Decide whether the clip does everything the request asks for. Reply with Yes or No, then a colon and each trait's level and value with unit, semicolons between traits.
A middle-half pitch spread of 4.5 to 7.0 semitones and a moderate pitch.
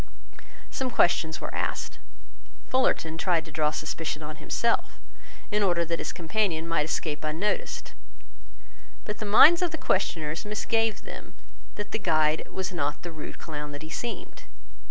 Yes: average, 5.1 semitones; medium, 165 Hz